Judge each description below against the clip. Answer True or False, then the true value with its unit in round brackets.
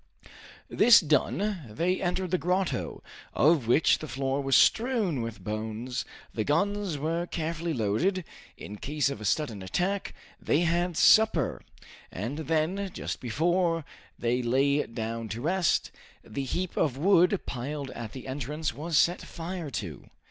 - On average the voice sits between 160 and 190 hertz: False (150 Hz)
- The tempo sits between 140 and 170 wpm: True (145 wpm)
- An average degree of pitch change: False (6.3 semitones)